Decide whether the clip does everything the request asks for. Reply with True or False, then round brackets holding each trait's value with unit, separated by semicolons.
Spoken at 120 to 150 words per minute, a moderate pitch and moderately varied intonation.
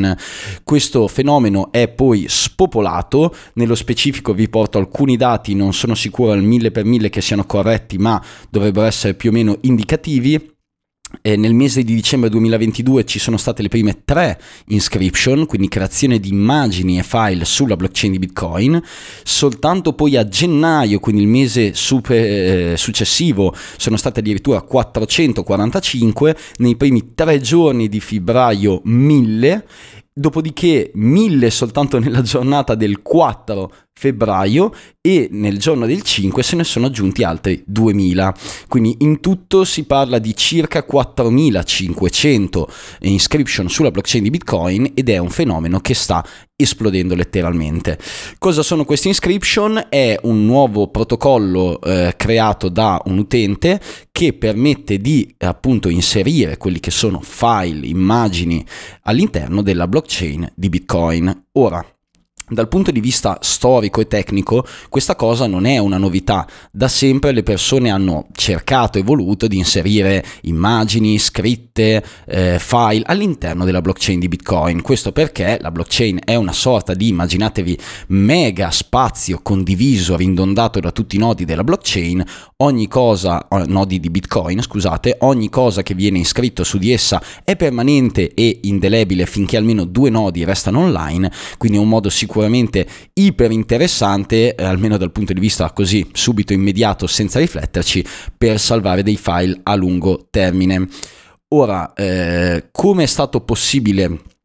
False (140 wpm; 110 Hz; 4.9 semitones)